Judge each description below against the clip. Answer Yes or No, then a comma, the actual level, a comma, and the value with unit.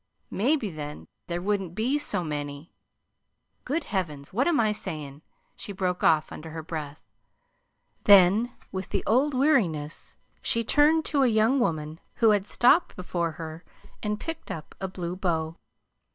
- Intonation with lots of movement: Yes, wide, 6.6 semitones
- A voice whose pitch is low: No, high, 190 Hz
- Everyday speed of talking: Yes, average, 150 wpm